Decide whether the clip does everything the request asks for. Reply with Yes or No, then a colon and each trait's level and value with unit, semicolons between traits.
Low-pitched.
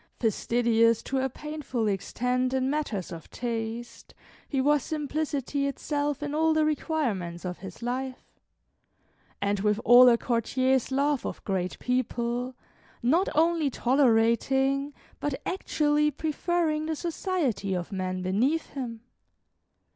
No: very high, 260 Hz